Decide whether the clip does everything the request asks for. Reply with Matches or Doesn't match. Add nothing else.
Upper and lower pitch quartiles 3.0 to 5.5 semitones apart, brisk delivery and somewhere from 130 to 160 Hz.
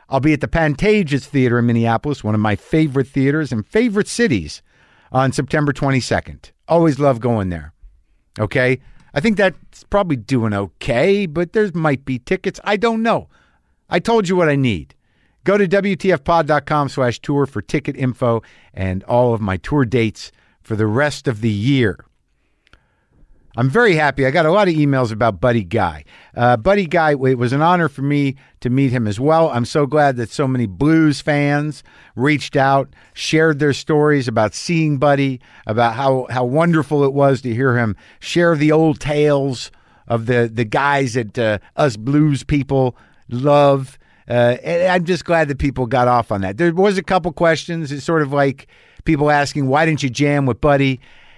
Doesn't match